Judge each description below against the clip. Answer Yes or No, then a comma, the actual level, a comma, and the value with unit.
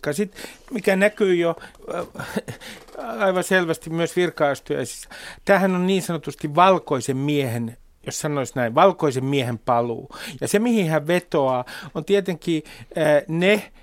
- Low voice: No, medium, 165 Hz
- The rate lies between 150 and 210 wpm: No, average, 125 wpm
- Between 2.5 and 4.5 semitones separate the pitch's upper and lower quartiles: No, average, 5.3 semitones